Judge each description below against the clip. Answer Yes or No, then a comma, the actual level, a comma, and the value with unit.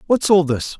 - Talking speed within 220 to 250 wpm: Yes, fast, 225 wpm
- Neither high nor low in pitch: Yes, medium, 170 Hz